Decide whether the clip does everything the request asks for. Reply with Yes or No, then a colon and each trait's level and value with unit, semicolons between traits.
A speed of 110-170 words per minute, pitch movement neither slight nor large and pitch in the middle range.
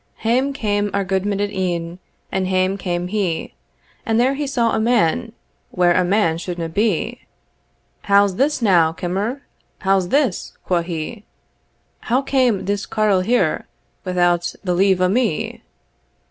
No: average, 145 wpm; average, 4.1 semitones; high, 195 Hz